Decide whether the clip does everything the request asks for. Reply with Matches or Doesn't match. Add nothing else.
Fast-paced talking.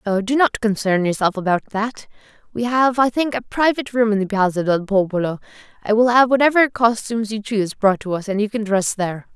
Matches